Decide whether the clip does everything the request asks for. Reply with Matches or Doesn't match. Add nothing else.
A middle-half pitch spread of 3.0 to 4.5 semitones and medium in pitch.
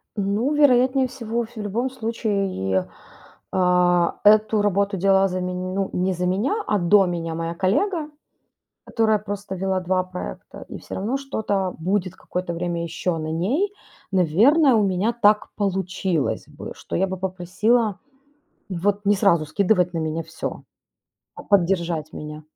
Doesn't match